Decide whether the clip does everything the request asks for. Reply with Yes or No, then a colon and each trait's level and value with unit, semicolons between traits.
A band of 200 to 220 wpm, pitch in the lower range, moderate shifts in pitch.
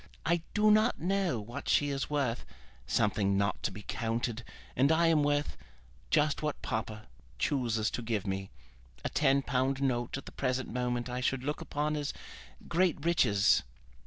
No: average, 165 wpm; low, 130 Hz; average, 4.7 semitones